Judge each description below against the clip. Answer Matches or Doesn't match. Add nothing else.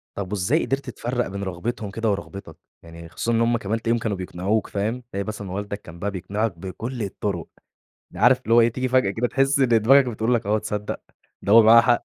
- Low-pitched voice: Matches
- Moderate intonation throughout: Matches